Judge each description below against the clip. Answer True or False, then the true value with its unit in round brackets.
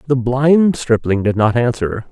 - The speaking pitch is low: True (125 Hz)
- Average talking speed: True (170 wpm)